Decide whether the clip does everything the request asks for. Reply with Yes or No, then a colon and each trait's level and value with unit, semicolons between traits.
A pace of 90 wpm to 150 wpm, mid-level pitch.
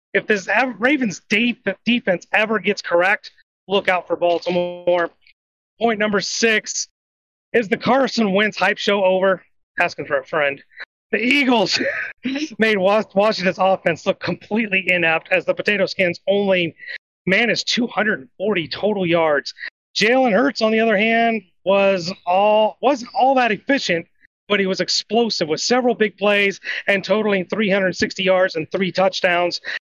No: average, 140 wpm; high, 195 Hz